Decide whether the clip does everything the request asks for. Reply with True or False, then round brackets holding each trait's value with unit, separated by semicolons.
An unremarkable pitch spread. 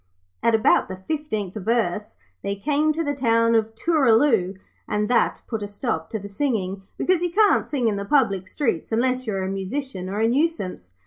False (6.1 semitones)